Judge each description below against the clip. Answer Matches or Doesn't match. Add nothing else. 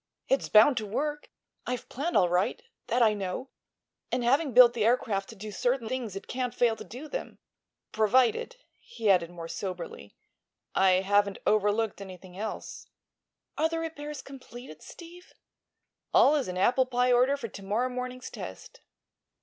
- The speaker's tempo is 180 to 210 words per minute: Doesn't match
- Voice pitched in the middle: Doesn't match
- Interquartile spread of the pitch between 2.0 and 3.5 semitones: Doesn't match